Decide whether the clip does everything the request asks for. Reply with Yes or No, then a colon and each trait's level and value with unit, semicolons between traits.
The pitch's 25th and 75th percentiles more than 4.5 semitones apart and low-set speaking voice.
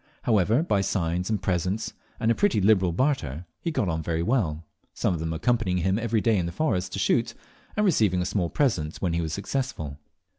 Yes: average, 5.2 semitones; very low, 95 Hz